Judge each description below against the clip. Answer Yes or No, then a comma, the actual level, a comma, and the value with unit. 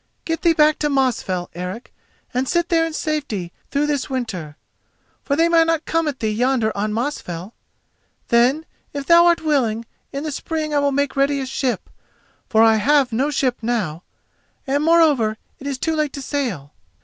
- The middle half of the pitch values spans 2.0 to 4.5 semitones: No, average, 5.3 semitones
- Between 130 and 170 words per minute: No, average, 185 wpm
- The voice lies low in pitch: No, very high, 275 Hz